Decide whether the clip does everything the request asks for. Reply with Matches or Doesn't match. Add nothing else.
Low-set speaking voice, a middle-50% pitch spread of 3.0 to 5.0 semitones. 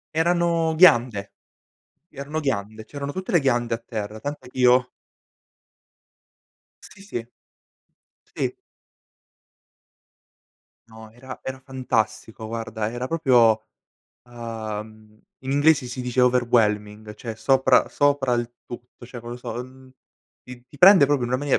Matches